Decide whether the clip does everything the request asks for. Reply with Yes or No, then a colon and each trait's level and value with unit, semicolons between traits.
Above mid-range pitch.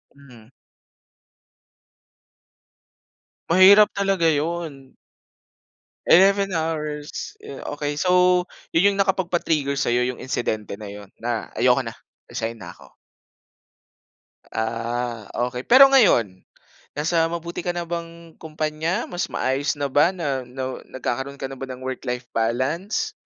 No: medium, 150 Hz